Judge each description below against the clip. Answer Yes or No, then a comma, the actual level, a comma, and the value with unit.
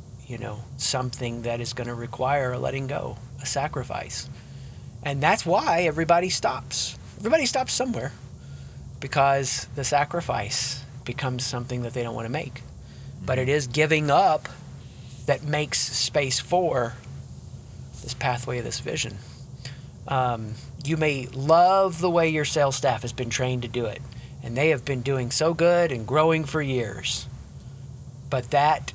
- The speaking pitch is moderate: No, low, 130 Hz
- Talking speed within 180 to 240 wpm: No, average, 155 wpm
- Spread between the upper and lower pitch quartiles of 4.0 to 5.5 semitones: No, average, 3.0 semitones